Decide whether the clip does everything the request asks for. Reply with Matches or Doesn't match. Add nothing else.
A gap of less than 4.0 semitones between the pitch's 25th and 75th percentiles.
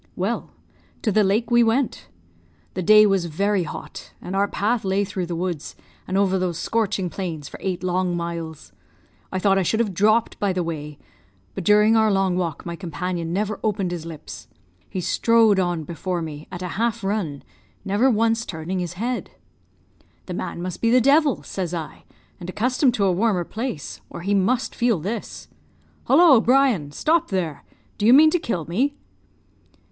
Doesn't match